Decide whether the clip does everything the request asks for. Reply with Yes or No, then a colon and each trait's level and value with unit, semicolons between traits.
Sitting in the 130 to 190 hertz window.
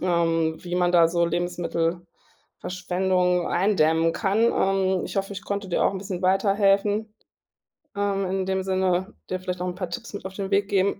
Yes: medium, 185 Hz